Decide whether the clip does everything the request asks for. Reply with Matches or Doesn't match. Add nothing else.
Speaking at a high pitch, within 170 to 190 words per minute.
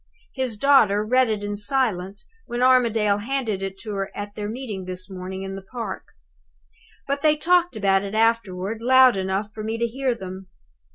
Matches